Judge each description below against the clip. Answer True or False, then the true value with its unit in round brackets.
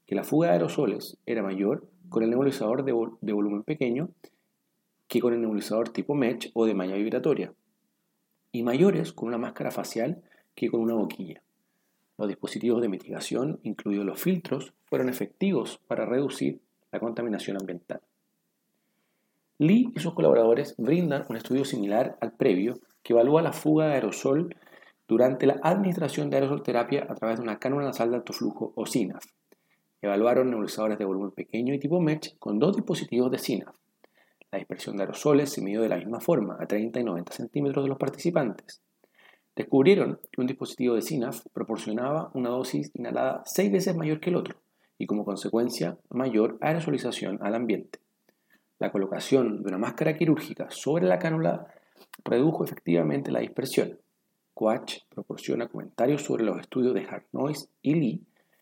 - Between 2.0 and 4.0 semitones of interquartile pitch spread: False (5.3 semitones)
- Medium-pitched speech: False (120 Hz)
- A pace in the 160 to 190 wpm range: True (165 wpm)